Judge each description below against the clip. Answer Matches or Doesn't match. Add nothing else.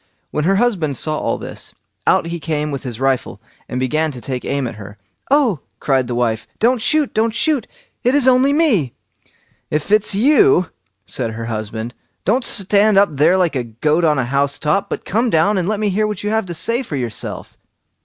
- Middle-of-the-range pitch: Matches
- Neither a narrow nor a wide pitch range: Doesn't match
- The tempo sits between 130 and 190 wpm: Doesn't match